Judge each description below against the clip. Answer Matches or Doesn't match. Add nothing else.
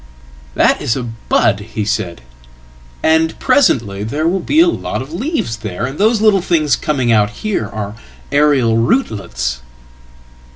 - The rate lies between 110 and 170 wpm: Matches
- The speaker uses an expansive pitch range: Matches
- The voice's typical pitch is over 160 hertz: Doesn't match